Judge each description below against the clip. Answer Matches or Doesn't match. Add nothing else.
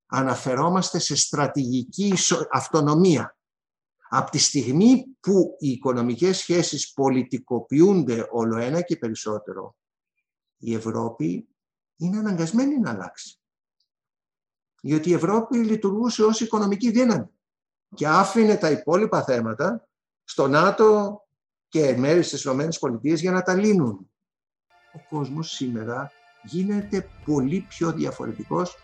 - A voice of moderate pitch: Matches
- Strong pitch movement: Matches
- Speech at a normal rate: Doesn't match